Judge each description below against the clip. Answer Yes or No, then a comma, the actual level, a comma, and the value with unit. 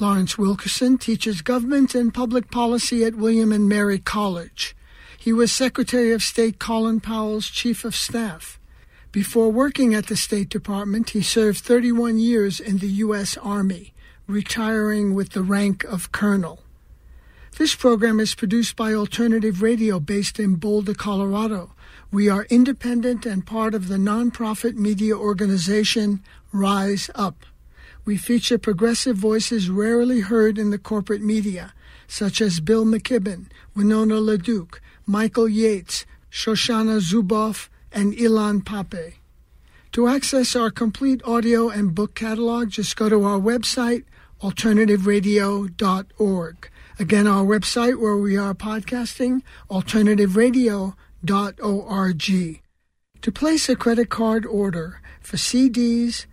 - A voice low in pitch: No, high, 215 Hz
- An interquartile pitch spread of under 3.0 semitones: Yes, narrow, 2.6 semitones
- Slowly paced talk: Yes, slow, 125 wpm